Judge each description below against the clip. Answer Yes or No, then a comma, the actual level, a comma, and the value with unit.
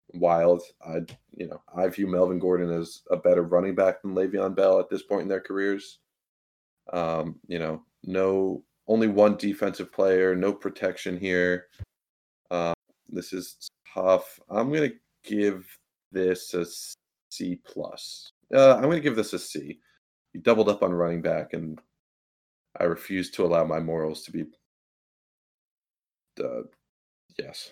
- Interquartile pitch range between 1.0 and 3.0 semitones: Yes, narrow, 2.5 semitones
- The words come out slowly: No, average, 150 wpm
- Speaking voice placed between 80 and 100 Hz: Yes, very low, 90 Hz